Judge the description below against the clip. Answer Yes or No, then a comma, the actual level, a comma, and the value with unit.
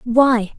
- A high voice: Yes, high, 240 Hz